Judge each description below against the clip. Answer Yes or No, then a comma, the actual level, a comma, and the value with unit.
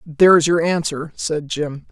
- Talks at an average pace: Yes, average, 155 wpm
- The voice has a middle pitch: Yes, medium, 160 Hz